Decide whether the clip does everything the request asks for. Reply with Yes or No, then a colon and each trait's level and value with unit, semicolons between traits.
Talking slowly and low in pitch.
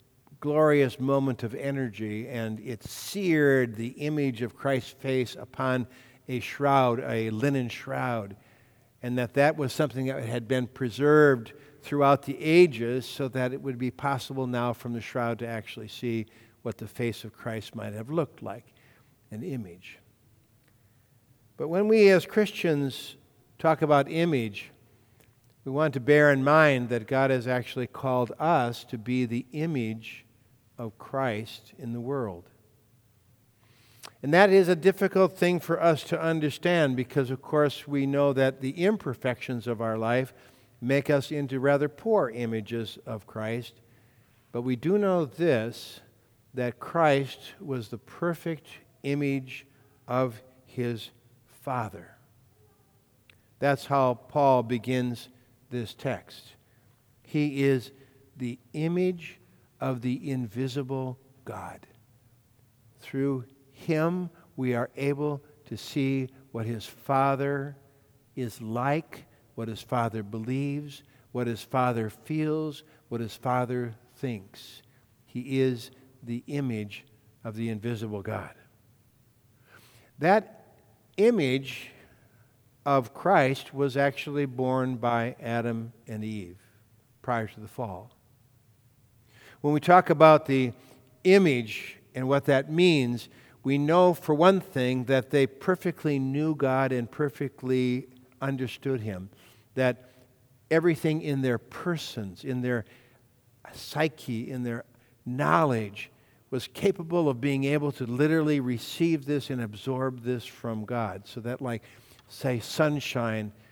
Yes: slow, 125 wpm; low, 125 Hz